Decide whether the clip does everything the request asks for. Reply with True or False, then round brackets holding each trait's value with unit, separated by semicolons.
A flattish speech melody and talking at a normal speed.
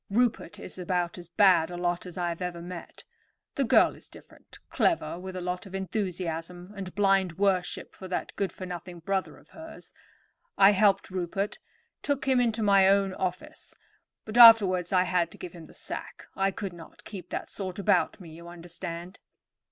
True (2.2 semitones; 185 wpm)